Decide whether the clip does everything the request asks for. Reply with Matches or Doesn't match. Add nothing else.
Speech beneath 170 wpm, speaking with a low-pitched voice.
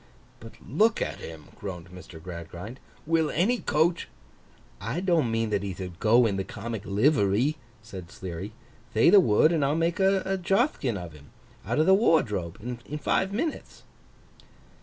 Matches